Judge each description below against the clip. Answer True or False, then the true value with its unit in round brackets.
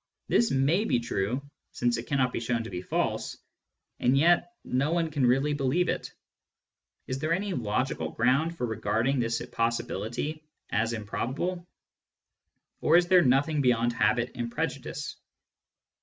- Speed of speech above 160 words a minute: False (145 wpm)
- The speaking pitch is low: True (130 Hz)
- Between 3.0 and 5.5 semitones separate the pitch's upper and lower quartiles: True (4.9 semitones)